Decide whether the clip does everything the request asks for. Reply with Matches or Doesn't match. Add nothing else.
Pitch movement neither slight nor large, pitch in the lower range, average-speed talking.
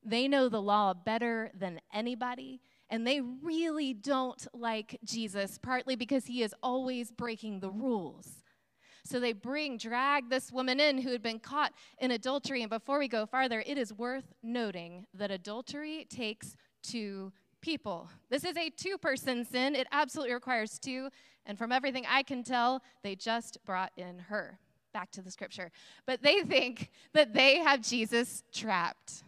Doesn't match